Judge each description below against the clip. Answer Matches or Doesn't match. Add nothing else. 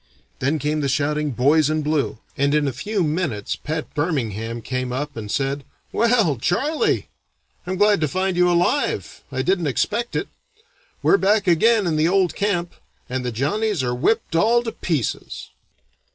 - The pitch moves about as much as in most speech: Doesn't match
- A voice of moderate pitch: Matches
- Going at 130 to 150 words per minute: Doesn't match